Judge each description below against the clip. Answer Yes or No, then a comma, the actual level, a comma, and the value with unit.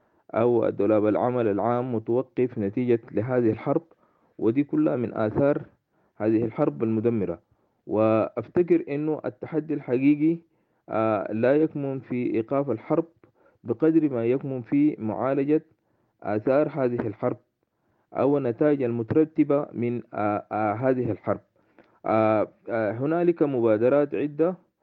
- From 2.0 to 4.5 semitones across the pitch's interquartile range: No, average, 5.1 semitones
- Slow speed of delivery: Yes, slow, 105 wpm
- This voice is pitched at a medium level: No, low, 125 Hz